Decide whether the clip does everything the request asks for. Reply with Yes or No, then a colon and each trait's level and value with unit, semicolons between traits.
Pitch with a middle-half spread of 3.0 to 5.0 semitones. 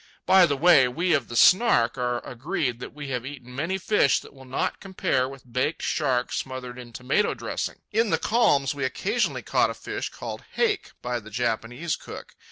No: wide, 5.6 semitones